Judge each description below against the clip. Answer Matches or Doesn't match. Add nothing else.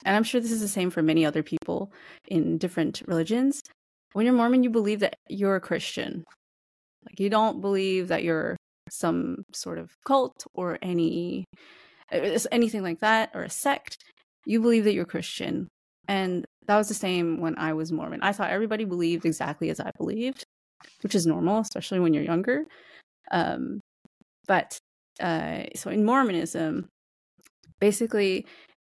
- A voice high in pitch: Matches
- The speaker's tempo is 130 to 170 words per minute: Matches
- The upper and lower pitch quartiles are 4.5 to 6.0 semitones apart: Matches